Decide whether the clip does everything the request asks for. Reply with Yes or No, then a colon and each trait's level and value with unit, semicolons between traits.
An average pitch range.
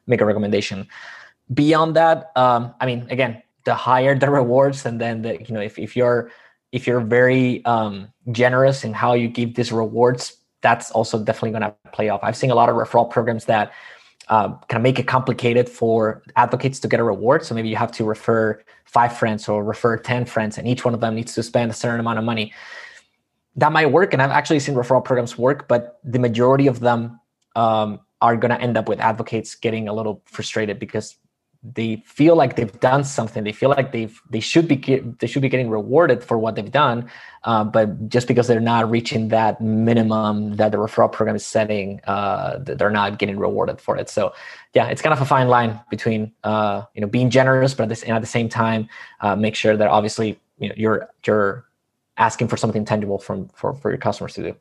No: narrow, 2.3 semitones